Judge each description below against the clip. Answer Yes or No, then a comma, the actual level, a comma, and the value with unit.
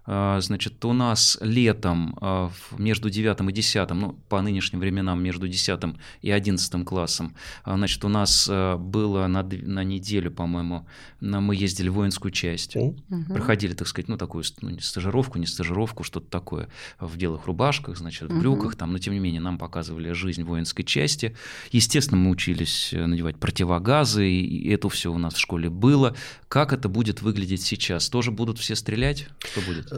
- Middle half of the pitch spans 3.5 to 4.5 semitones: Yes, average, 3.9 semitones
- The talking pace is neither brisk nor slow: No, fast, 165 wpm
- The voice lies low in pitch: Yes, very low, 95 Hz